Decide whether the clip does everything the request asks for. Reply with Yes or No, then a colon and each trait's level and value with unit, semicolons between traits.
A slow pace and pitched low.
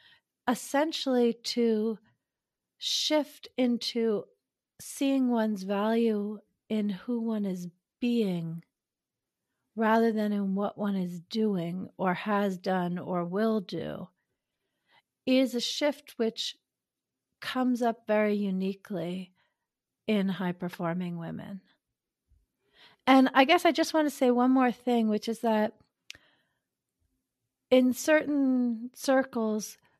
No: slow, 110 wpm; high, 220 Hz